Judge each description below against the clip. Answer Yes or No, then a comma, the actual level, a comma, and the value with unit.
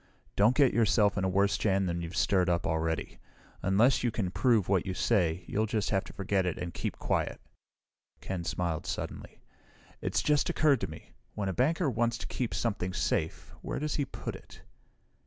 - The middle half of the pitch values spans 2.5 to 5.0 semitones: Yes, average, 4.7 semitones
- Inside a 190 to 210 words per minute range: Yes, average, 195 wpm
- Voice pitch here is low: Yes, low, 100 Hz